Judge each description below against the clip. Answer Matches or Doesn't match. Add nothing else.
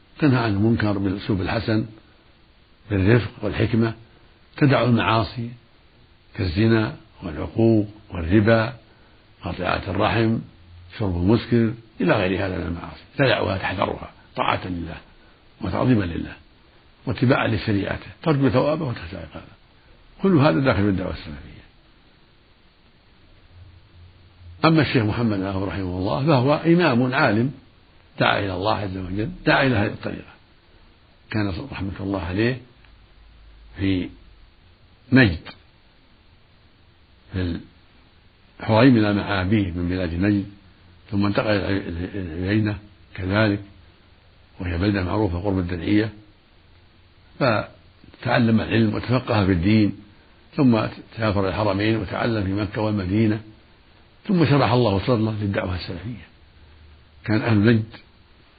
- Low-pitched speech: Matches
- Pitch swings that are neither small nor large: Matches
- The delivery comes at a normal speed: Matches